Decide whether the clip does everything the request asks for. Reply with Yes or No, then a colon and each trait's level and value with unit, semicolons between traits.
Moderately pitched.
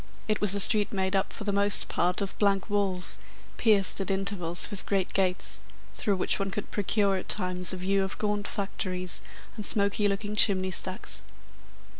No: high, 195 Hz